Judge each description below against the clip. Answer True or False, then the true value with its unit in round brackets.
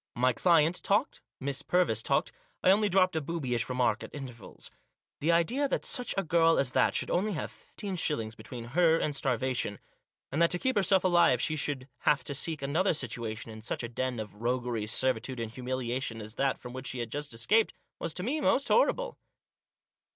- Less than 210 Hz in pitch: True (135 Hz)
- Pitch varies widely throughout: True (6.2 semitones)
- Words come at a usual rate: True (195 wpm)